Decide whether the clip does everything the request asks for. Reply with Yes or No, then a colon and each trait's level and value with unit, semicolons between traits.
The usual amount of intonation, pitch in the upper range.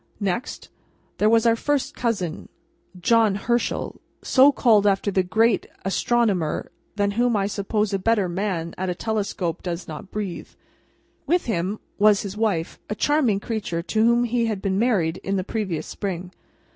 Yes: average, 3.5 semitones; high, 205 Hz